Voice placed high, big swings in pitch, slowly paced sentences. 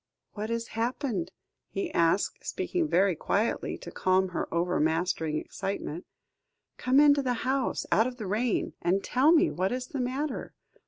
No: high, 220 Hz; wide, 5.8 semitones; average, 155 wpm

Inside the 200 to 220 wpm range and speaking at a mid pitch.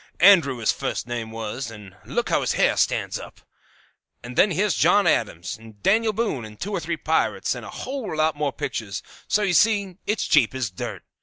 Yes: fast, 205 wpm; medium, 150 Hz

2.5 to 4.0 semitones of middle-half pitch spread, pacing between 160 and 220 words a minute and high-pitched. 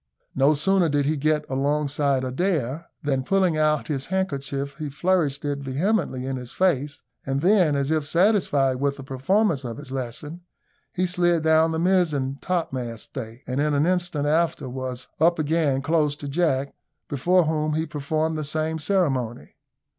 No: average, 3.5 semitones; average, 165 wpm; medium, 150 Hz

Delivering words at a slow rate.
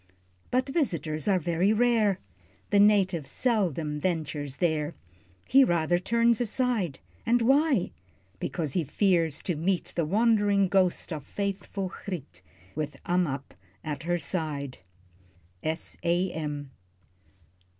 Yes: slow, 120 wpm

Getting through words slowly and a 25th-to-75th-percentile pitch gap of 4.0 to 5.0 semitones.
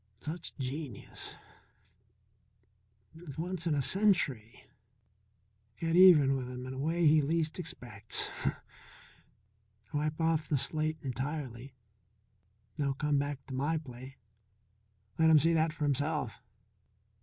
No: slow, 115 wpm; average, 3.4 semitones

